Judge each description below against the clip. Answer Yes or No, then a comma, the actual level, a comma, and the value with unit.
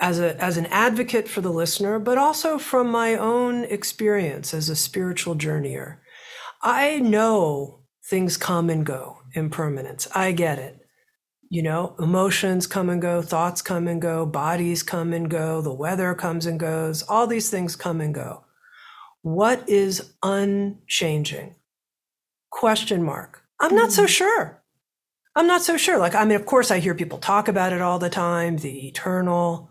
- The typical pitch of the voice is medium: Yes, medium, 180 Hz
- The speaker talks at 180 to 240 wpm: No, average, 165 wpm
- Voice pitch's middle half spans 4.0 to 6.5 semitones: Yes, average, 4.7 semitones